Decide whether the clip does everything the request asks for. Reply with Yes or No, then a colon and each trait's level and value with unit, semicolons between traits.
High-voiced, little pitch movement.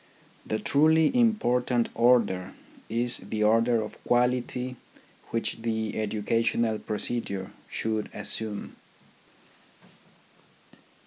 No: low, 115 Hz; narrow, 2.3 semitones